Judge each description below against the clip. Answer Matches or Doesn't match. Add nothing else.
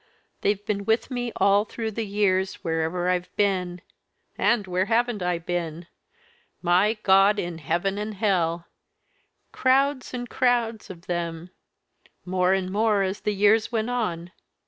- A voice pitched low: Doesn't match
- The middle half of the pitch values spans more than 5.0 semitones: Doesn't match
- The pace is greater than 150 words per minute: Doesn't match